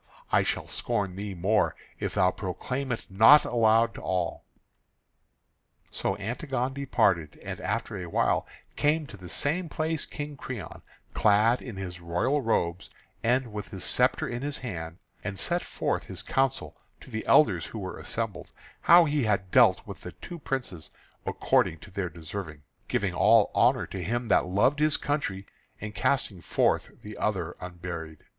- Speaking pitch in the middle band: No, low, 105 Hz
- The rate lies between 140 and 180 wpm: Yes, average, 165 wpm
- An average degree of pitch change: No, wide, 6.3 semitones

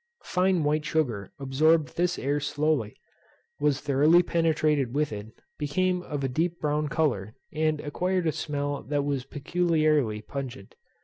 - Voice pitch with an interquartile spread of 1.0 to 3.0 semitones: Yes, narrow, 2.6 semitones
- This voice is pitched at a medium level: Yes, medium, 150 Hz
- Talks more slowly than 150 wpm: Yes, average, 140 wpm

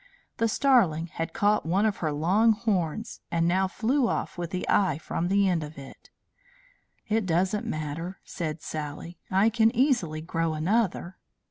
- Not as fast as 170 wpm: Yes, average, 160 wpm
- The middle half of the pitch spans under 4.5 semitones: No, average, 4.9 semitones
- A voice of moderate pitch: Yes, medium, 180 Hz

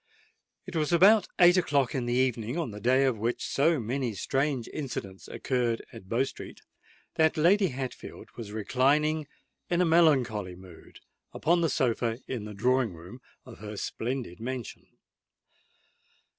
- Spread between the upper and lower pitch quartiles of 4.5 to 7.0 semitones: Yes, average, 5.2 semitones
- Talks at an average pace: Yes, average, 150 wpm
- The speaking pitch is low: Yes, low, 130 Hz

